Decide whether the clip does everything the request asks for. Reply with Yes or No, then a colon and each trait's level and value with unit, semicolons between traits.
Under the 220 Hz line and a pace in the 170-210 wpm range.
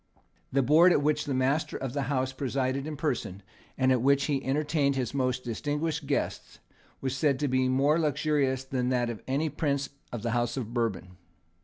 Yes: low, 135 Hz; average, 190 wpm